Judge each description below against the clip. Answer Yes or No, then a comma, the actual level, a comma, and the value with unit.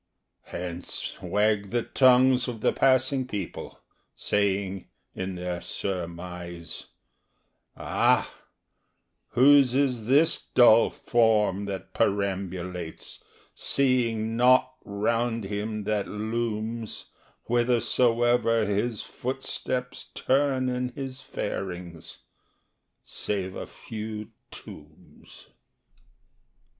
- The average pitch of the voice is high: No, low, 110 Hz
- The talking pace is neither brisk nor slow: No, slow, 80 wpm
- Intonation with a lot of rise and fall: No, average, 4.1 semitones